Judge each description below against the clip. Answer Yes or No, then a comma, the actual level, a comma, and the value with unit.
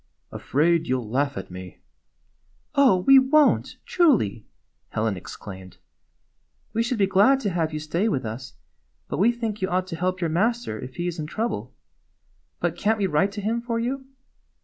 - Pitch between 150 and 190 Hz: Yes, medium, 185 Hz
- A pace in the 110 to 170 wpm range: No, average, 185 wpm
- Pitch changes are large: Yes, wide, 8.7 semitones